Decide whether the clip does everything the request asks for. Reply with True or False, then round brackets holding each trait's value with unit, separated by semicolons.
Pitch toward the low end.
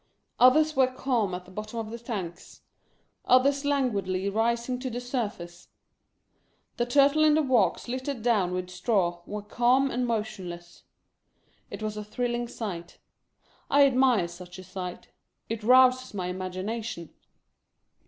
False (225 Hz)